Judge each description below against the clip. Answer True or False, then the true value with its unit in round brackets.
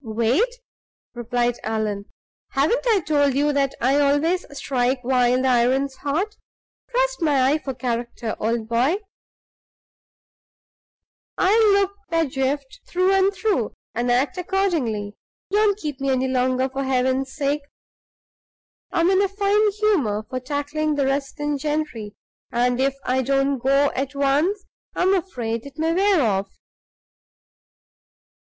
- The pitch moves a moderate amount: False (5.8 semitones)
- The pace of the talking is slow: True (130 wpm)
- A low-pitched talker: False (275 Hz)